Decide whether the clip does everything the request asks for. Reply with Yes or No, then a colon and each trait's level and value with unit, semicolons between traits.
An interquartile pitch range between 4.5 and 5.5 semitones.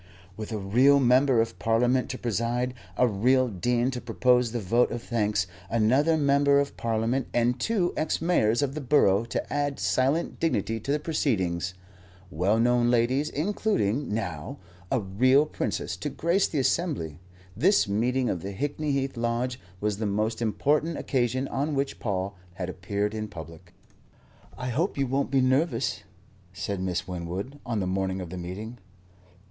Yes: average, 5.0 semitones